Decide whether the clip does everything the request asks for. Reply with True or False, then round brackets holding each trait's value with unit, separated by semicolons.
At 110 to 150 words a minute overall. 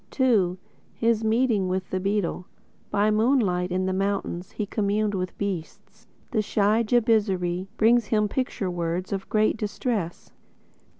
True (135 wpm)